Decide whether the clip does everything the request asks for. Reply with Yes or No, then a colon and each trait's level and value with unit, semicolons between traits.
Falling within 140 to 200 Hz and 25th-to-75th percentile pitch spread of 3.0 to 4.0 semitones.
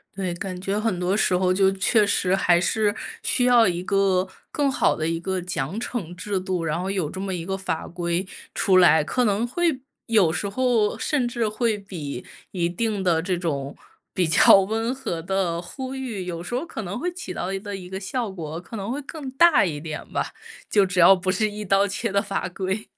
Yes: high, 195 Hz; average, 3.7 semitones